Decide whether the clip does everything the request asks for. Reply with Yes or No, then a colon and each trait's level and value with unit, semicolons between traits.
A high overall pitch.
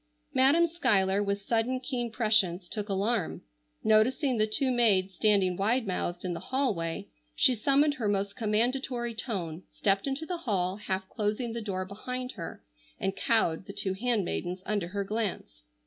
Yes: high, 215 Hz